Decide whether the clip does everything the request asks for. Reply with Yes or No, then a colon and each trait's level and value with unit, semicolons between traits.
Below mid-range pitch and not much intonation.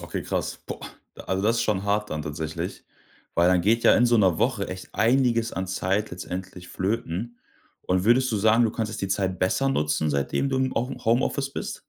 No: low, 105 Hz; average, 4.2 semitones